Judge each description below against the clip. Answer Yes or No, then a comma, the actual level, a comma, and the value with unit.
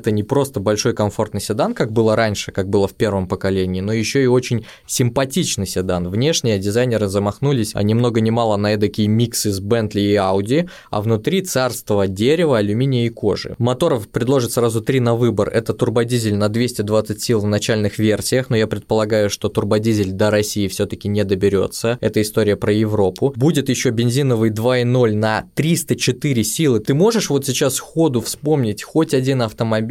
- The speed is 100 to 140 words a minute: No, average, 175 wpm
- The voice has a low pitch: Yes, low, 110 Hz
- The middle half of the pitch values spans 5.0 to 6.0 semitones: No, average, 3.3 semitones